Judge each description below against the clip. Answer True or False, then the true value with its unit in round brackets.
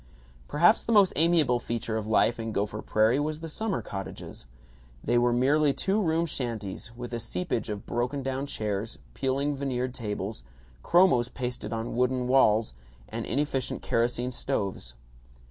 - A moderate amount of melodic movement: True (4.3 semitones)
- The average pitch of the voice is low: True (125 Hz)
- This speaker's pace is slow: False (150 wpm)